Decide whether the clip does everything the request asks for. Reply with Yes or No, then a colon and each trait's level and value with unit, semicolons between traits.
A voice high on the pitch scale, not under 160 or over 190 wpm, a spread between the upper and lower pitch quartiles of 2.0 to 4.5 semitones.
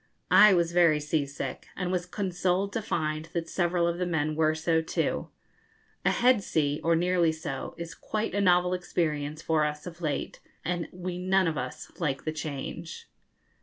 No: medium, 170 Hz; average, 180 wpm; narrow, 2.6 semitones